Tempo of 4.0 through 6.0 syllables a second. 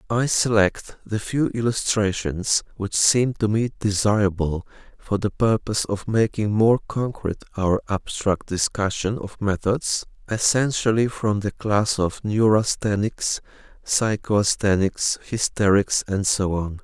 Yes: 4.1 syllables/s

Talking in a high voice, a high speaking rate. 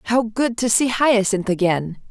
No: high, 220 Hz; average, 170 wpm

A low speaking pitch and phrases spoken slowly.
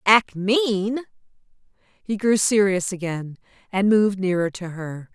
No: high, 200 Hz; slow, 130 wpm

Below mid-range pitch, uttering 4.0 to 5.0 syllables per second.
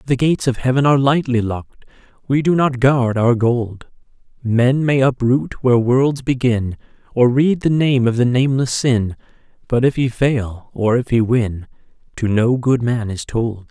Yes: low, 125 Hz; 4.6 syllables/s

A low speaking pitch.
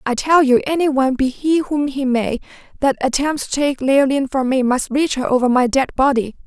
No: very high, 270 Hz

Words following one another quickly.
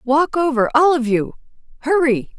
No: slow, 100 wpm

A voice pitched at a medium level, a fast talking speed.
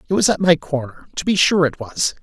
Yes: medium, 160 Hz; fast, 270 wpm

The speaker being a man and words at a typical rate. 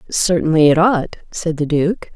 No: female; average, 165 wpm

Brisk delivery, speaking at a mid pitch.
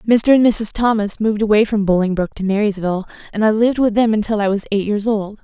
No: fast, 230 wpm; high, 210 Hz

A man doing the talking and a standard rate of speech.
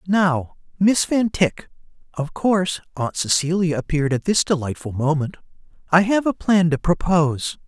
Yes: male; average, 150 wpm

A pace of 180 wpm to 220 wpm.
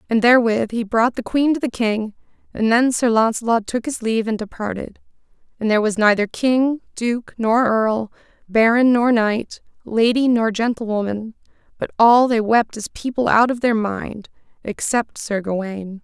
No: average, 170 wpm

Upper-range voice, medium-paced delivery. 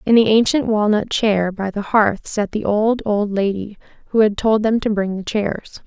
No: high, 210 Hz; fast, 215 wpm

